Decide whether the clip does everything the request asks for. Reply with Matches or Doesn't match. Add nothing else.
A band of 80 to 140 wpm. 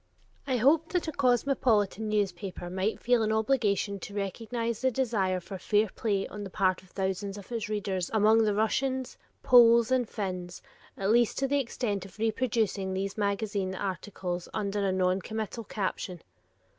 Doesn't match